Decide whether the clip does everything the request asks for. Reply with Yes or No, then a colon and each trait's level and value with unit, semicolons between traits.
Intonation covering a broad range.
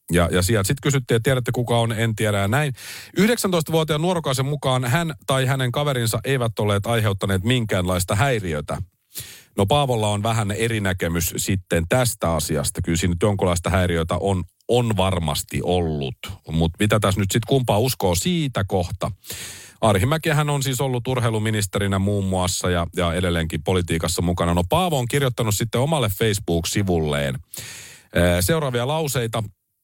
Yes: wide, 6.1 semitones